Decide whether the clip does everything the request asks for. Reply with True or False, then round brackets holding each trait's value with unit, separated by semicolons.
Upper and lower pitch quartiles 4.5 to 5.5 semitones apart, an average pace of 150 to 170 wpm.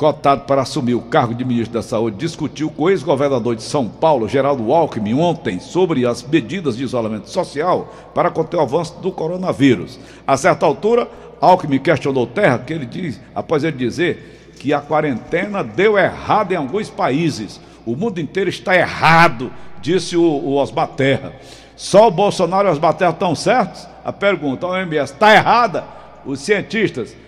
True (5.1 semitones; 165 wpm)